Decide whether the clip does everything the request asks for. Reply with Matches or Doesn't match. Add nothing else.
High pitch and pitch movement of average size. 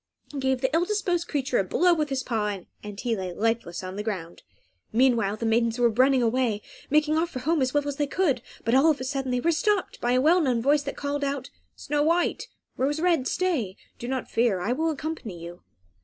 Matches